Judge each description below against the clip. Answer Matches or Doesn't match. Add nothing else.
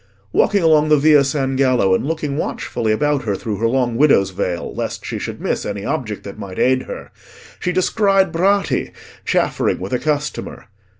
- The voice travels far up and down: Matches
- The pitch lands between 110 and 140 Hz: Matches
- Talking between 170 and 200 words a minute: Matches